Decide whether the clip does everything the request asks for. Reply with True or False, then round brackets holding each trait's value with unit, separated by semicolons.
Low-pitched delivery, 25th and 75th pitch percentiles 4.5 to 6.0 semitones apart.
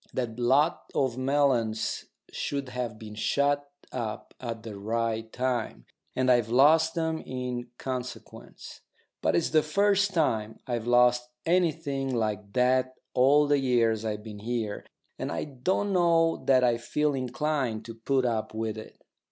False (125 Hz; 4.1 semitones)